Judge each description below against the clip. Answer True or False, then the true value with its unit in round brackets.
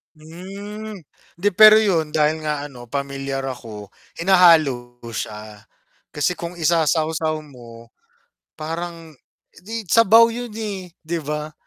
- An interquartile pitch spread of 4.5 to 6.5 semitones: True (4.9 semitones)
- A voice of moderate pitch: True (155 Hz)